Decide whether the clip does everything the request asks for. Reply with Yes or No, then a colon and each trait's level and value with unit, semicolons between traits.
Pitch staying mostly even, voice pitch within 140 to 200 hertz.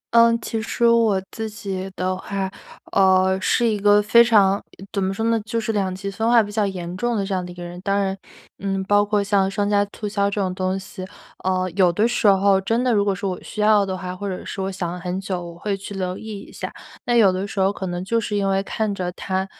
Yes: narrow, 1.9 semitones; high, 195 Hz